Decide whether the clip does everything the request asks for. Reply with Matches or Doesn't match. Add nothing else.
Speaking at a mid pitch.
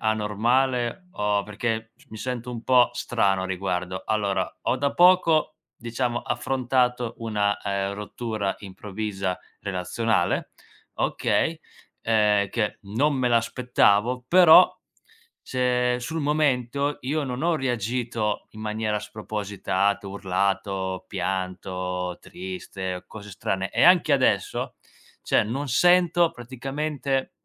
Doesn't match